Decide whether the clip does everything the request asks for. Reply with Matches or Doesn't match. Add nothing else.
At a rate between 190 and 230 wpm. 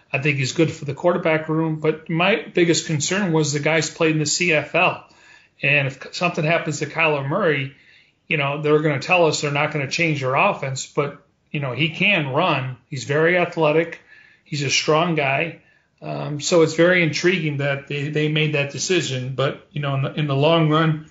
Matches